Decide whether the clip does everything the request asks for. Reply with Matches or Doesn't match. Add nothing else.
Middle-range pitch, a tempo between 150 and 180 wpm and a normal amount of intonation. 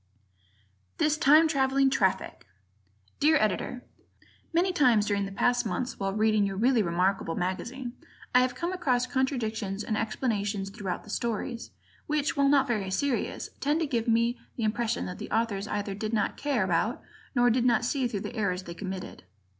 Doesn't match